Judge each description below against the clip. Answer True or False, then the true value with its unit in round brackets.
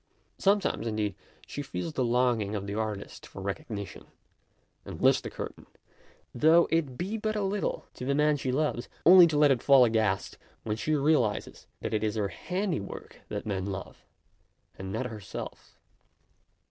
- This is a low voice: True (125 Hz)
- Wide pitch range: True (6.6 semitones)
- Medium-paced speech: True (170 wpm)